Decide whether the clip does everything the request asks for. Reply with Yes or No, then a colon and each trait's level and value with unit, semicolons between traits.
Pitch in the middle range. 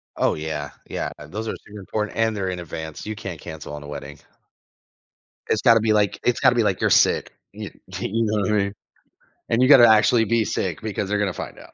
No: low, 105 Hz